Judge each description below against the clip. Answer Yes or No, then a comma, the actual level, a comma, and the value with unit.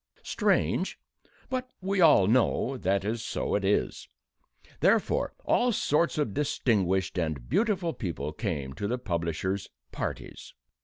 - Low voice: Yes, low, 105 Hz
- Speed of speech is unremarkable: No, slow, 120 wpm